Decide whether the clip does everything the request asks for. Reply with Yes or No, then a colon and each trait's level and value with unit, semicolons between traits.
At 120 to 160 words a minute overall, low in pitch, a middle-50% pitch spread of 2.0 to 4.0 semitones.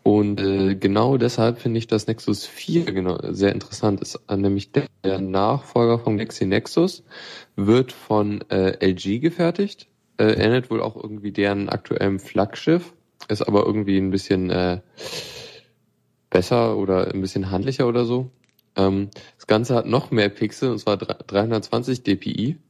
Yes: average, 155 wpm; low, 105 Hz; average, 3.5 semitones